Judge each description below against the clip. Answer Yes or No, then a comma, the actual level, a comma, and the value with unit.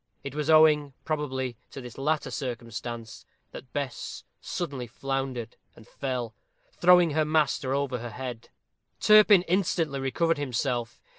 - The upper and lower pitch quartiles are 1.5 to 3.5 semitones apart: No, average, 4.0 semitones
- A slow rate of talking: Yes, slow, 130 wpm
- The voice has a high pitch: No, low, 135 Hz